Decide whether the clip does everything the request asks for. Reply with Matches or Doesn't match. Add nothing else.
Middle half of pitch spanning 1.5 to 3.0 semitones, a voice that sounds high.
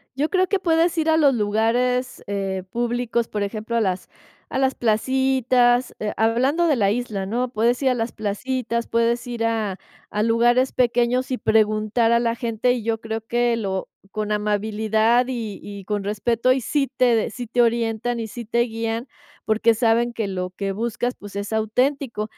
Matches